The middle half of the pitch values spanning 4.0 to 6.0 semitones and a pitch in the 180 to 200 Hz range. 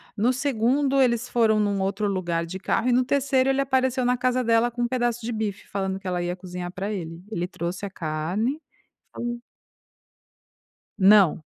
No: average, 4.9 semitones; high, 220 Hz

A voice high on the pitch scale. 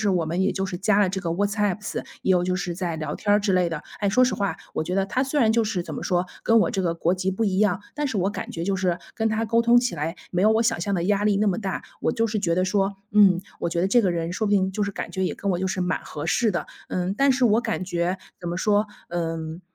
Yes: high, 195 Hz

